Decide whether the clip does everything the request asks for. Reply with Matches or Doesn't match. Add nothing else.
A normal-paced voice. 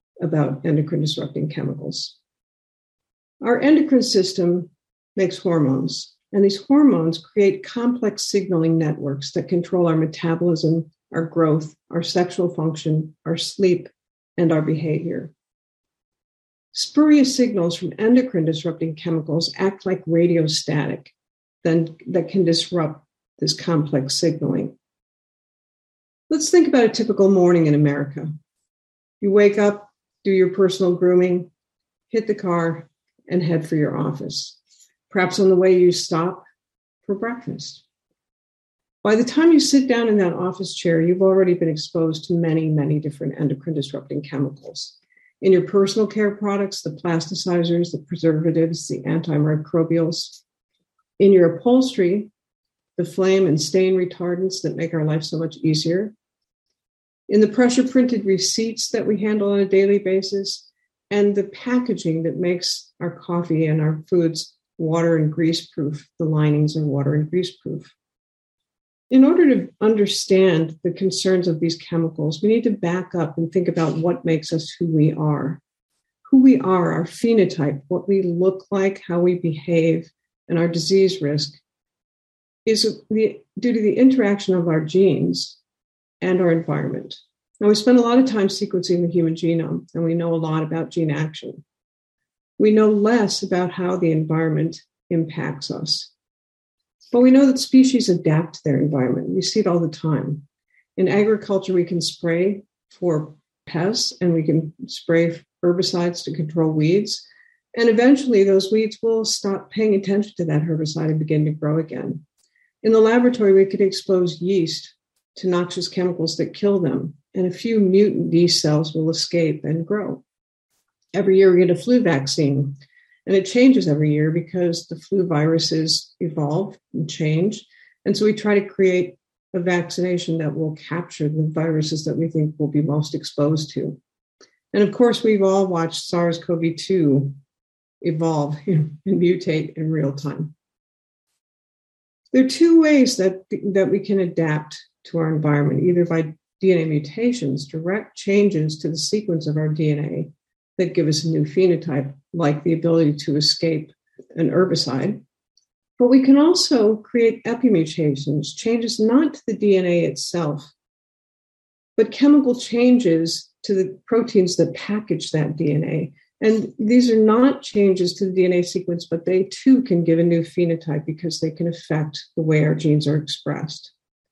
Matches